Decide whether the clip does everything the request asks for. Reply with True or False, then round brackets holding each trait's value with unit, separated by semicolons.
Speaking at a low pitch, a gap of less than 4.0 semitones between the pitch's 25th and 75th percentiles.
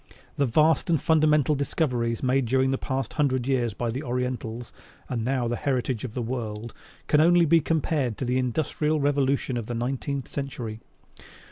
True (130 Hz; 3.2 semitones)